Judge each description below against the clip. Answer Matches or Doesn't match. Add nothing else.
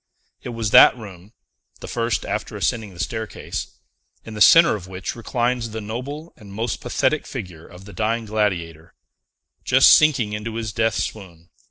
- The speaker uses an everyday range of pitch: Matches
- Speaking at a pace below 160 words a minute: Doesn't match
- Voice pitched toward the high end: Doesn't match